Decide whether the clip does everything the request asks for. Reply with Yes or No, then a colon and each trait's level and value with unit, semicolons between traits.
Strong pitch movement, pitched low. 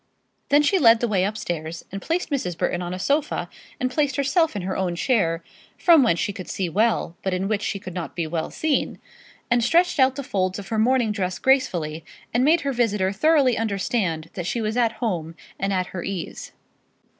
No: wide, 6.1 semitones; high, 210 Hz